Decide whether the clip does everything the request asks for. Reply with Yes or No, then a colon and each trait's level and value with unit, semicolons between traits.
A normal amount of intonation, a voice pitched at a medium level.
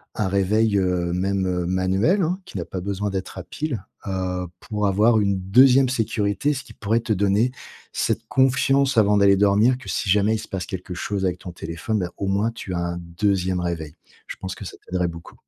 No: average, 3.3 semitones; low, 100 Hz